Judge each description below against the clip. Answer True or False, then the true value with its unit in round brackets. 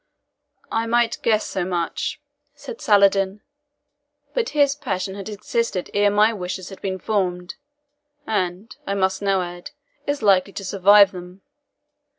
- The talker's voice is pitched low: False (195 Hz)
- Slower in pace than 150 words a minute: True (140 wpm)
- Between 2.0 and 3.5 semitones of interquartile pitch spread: True (2.6 semitones)